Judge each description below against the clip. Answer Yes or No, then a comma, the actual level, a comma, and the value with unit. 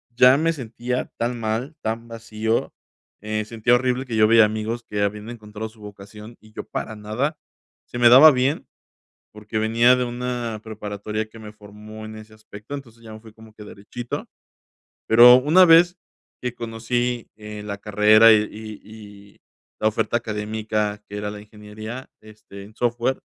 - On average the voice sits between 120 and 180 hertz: No, low, 110 Hz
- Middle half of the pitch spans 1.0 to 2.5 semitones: Yes, narrow, 2.2 semitones